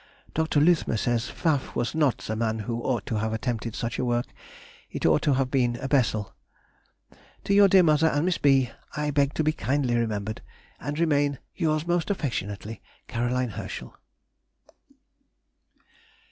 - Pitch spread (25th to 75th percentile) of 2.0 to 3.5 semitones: No, average, 4.7 semitones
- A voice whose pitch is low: Yes, low, 130 Hz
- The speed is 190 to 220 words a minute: No, average, 160 wpm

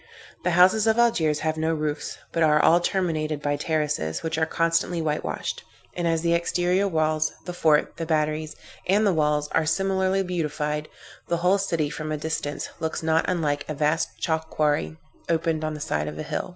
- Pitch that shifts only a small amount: Yes, narrow, 2.3 semitones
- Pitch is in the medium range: Yes, medium, 160 Hz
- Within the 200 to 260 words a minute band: No, average, 190 wpm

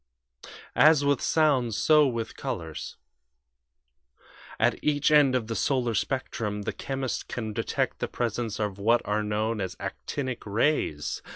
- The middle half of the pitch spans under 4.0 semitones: No, average, 4.5 semitones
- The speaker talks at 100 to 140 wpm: Yes, slow, 135 wpm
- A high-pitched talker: No, low, 120 Hz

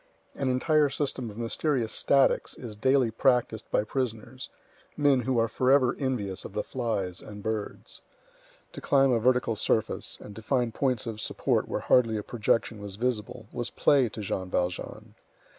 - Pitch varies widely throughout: No, average, 3.4 semitones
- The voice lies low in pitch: Yes, low, 120 Hz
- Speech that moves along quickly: No, average, 165 wpm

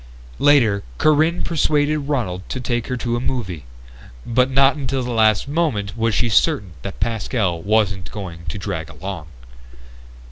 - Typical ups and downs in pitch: No, wide, 5.8 semitones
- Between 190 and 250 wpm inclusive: No, average, 150 wpm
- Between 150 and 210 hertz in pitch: No, low, 115 Hz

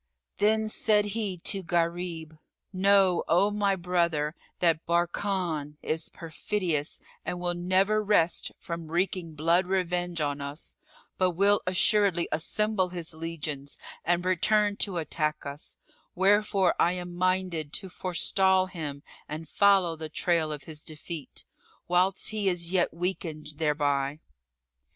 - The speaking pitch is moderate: Yes, medium, 175 Hz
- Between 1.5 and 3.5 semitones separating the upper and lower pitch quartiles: Yes, average, 3.1 semitones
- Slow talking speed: Yes, slow, 130 wpm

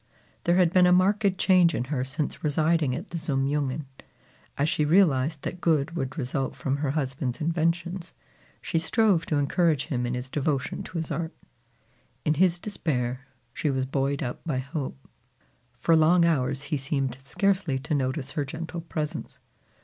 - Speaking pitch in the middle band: Yes, medium, 150 Hz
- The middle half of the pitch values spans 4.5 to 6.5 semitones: No, average, 3.9 semitones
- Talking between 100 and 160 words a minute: No, average, 170 wpm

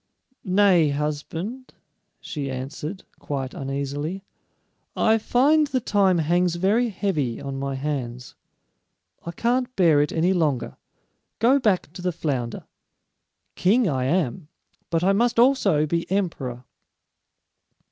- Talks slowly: Yes, slow, 120 wpm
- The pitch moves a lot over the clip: Yes, wide, 6.2 semitones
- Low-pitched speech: No, medium, 170 Hz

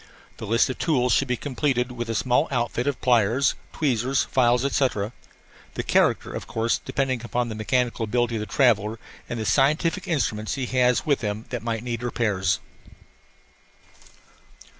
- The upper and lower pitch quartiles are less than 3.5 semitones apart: Yes, average, 2.7 semitones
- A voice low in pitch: Yes, low, 120 Hz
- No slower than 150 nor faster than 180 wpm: Yes, average, 160 wpm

